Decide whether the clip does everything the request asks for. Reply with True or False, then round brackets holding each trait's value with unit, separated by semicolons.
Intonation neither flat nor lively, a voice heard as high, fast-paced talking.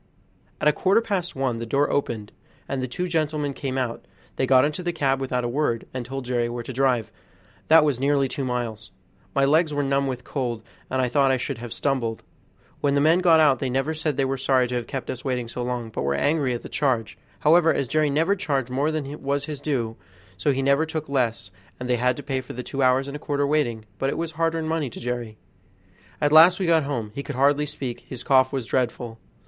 False (3.2 semitones; 135 Hz; 245 wpm)